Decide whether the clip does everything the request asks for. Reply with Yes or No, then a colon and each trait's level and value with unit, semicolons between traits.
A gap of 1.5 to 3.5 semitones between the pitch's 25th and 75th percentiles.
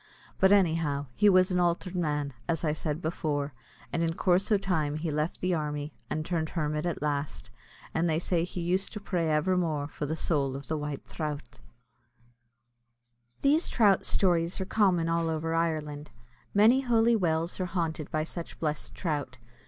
Yes: average, 3.2 semitones